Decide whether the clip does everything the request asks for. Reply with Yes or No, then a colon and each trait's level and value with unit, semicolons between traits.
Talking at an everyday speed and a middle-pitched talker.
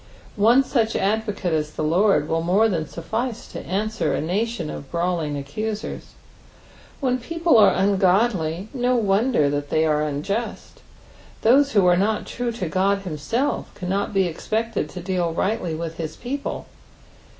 No: average, 155 wpm; high, 195 Hz